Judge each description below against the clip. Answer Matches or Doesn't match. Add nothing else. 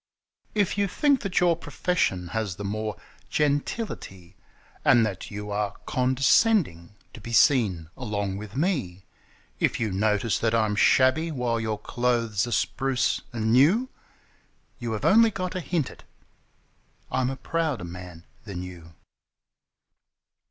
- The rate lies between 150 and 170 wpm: Doesn't match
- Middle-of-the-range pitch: Doesn't match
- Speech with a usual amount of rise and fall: Doesn't match